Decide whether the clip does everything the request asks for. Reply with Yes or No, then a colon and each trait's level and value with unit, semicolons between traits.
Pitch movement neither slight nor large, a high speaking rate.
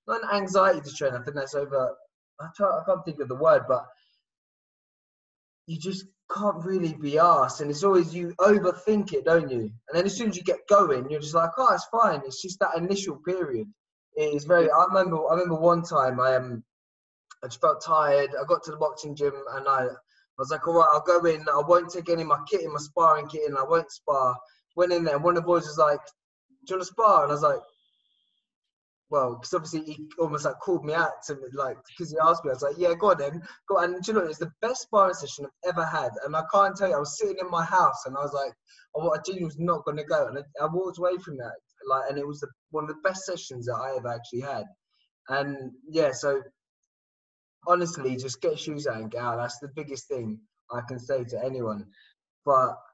Yes: average, 4.5 semitones; fast, 245 wpm